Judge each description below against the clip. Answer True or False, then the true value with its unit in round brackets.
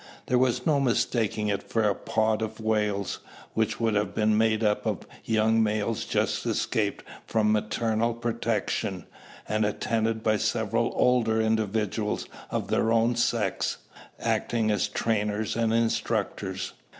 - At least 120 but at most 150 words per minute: True (140 wpm)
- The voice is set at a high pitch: False (110 Hz)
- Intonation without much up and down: True (1.3 semitones)